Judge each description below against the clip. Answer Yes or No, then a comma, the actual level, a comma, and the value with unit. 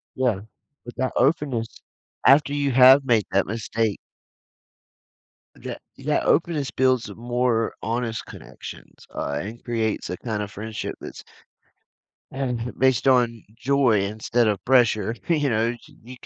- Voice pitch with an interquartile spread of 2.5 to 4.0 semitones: Yes, average, 2.9 semitones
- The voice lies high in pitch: No, low, 120 Hz